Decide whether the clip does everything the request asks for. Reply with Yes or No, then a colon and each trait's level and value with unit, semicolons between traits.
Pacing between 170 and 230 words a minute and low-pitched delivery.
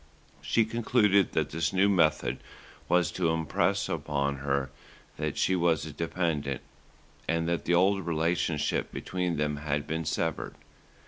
No: average, 140 wpm; very low, 80 Hz